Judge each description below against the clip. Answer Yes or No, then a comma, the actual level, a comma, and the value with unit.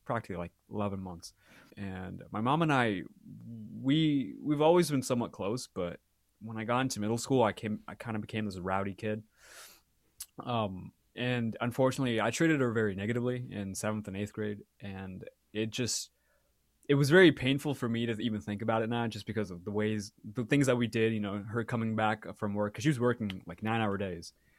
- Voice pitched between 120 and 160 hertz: No, low, 110 Hz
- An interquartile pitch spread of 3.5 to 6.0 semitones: No, average, 3.1 semitones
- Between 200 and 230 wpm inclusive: Yes, fast, 205 wpm